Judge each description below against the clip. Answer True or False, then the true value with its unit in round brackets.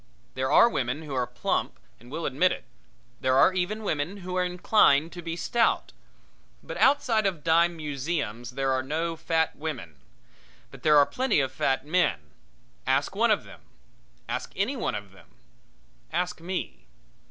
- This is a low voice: False (160 Hz)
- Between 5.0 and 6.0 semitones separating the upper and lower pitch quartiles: True (5.4 semitones)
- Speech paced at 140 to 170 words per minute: True (165 wpm)